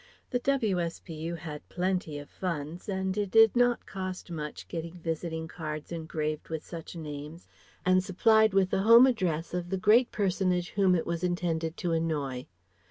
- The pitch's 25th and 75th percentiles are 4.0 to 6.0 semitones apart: No, average, 3.0 semitones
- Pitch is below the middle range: No, medium, 175 Hz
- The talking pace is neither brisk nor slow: Yes, average, 165 wpm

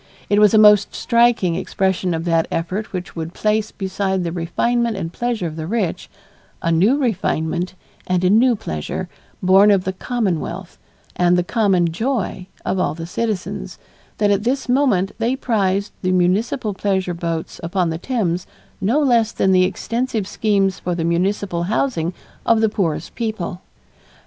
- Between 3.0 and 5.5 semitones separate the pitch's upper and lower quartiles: Yes, average, 3.9 semitones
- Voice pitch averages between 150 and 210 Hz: Yes, high, 190 Hz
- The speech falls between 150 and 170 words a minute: Yes, average, 165 wpm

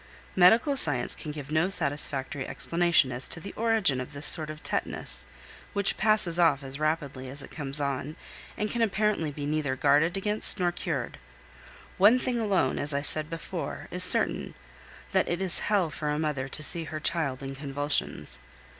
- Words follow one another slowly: No, average, 180 wpm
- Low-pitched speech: No, medium, 155 Hz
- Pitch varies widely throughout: No, average, 4.7 semitones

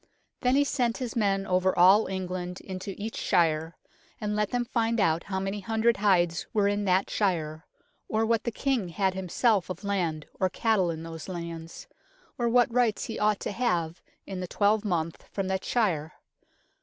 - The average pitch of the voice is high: Yes, high, 195 Hz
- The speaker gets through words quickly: No, average, 180 wpm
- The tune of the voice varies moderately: Yes, average, 3.8 semitones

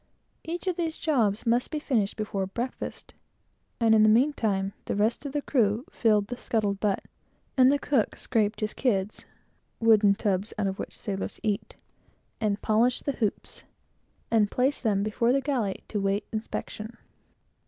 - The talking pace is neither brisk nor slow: Yes, average, 165 wpm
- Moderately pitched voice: No, high, 220 Hz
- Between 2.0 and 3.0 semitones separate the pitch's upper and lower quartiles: No, average, 3.6 semitones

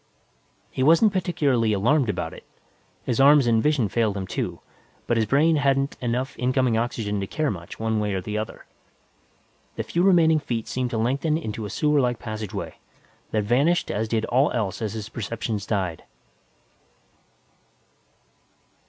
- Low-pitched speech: Yes, low, 120 Hz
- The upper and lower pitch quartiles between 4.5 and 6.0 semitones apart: Yes, average, 4.8 semitones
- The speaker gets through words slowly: No, average, 155 wpm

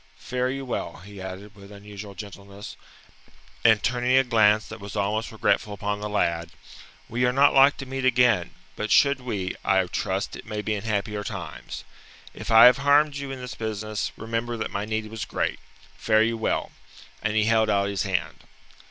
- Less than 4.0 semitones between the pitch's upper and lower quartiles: Yes, average, 3.3 semitones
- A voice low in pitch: Yes, low, 110 Hz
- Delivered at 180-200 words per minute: Yes, average, 190 wpm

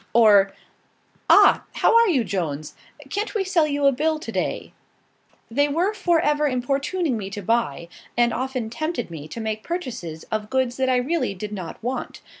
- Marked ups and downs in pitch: Yes, wide, 6.5 semitones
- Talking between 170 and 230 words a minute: Yes, average, 180 wpm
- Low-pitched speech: No, very high, 255 Hz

